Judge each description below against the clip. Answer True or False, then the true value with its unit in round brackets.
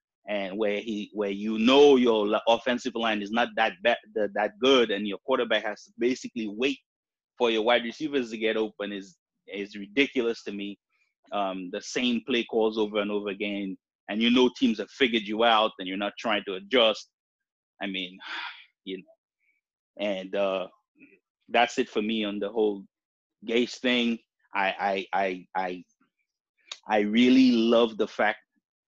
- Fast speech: False (170 wpm)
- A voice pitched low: True (110 Hz)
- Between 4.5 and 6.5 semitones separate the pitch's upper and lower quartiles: False (3.0 semitones)